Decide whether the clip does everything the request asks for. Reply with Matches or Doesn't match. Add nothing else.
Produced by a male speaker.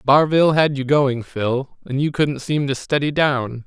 Matches